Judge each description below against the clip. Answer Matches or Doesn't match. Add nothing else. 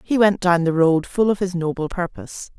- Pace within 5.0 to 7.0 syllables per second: Matches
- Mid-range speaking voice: Matches